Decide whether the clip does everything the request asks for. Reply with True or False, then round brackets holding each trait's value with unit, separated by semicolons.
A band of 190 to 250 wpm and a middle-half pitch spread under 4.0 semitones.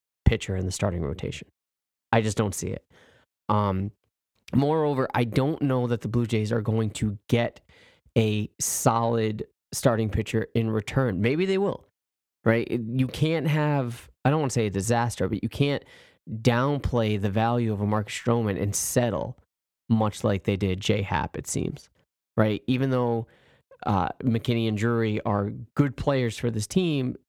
False (165 wpm; 3.3 semitones)